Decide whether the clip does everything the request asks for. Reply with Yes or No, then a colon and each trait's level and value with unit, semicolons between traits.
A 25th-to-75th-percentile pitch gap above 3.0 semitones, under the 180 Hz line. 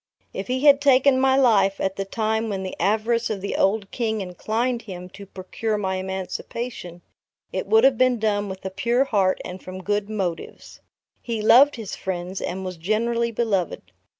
No: average, 3.8 semitones; high, 210 Hz